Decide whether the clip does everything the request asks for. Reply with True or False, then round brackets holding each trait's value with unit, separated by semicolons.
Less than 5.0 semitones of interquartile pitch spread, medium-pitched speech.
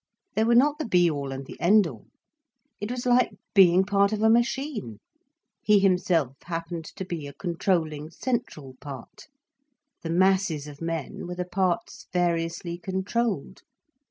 True (4.2 semitones; 180 Hz)